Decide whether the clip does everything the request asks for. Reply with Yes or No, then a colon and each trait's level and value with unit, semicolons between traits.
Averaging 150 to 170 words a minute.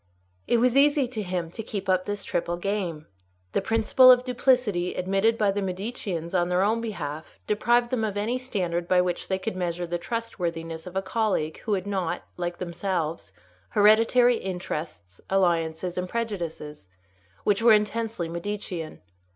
Yes: average, 160 wpm